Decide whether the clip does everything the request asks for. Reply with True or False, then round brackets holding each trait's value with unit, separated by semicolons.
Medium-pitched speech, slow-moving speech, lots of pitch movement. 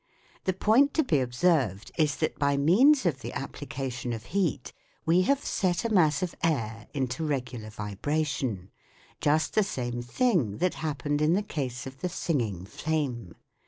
False (145 Hz; 165 wpm; 6.3 semitones)